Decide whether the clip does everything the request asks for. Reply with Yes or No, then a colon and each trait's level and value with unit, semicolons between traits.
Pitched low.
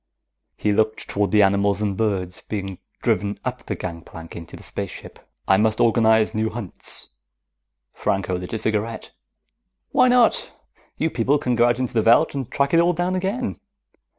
Yes: low, 110 Hz